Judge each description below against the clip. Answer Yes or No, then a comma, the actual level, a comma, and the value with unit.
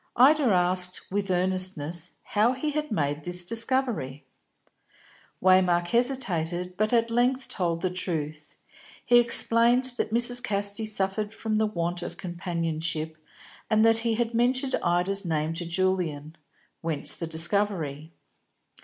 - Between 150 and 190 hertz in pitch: Yes, medium, 185 Hz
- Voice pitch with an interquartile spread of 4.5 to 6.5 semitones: Yes, average, 5.2 semitones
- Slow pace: Yes, slow, 130 wpm